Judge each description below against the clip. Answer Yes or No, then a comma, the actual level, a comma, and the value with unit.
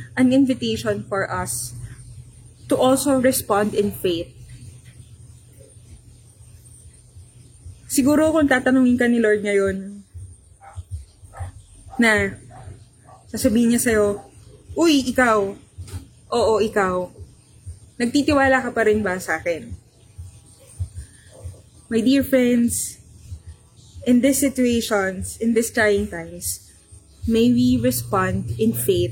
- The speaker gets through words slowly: Yes, slow, 95 wpm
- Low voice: Yes, low, 125 Hz